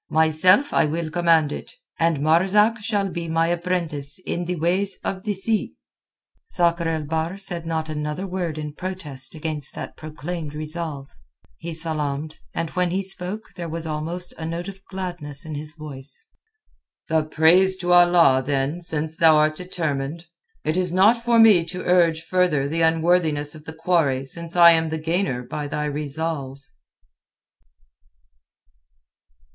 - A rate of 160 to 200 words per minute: No, average, 150 wpm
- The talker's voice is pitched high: No, medium, 165 Hz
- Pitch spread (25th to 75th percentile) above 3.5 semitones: No, average, 2.7 semitones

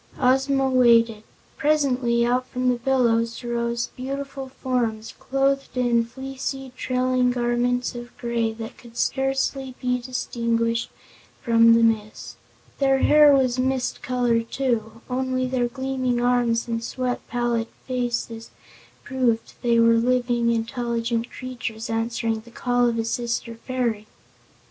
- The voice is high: Yes, high, 245 Hz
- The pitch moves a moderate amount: No, narrow, 1.8 semitones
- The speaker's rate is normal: No, slow, 125 wpm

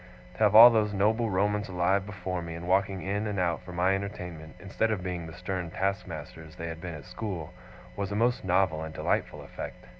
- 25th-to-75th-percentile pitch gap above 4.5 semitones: No, average, 2.9 semitones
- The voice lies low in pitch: Yes, very low, 95 Hz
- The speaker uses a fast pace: Yes, fast, 210 wpm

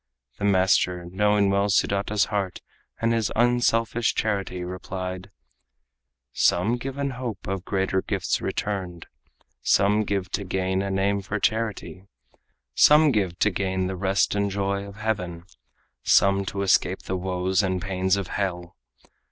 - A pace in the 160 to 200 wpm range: No, average, 145 wpm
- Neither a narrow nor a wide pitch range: No, narrow, 2.0 semitones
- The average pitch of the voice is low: Yes, low, 100 Hz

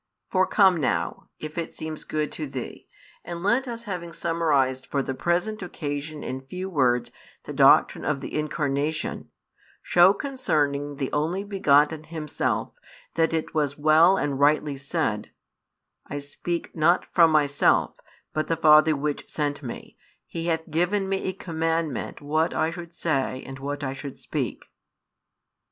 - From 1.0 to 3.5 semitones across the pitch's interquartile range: Yes, average, 3.1 semitones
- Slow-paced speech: No, average, 150 wpm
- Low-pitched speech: No, medium, 155 Hz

